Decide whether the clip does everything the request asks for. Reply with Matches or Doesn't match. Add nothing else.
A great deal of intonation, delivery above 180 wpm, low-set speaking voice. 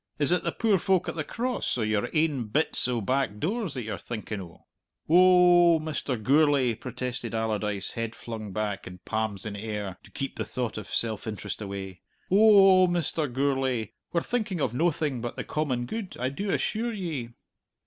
Matches